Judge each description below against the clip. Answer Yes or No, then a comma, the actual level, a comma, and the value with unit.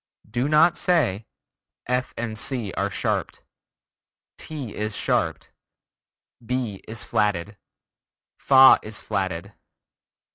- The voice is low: Yes, low, 110 Hz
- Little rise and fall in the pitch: No, average, 4.2 semitones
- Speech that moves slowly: Yes, slow, 100 wpm